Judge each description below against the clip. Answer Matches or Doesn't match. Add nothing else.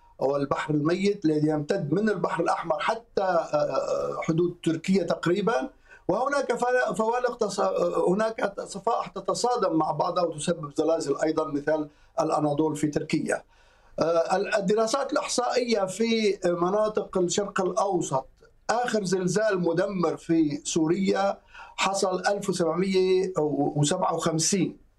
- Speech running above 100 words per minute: Doesn't match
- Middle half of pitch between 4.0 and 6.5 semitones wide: Matches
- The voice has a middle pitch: Matches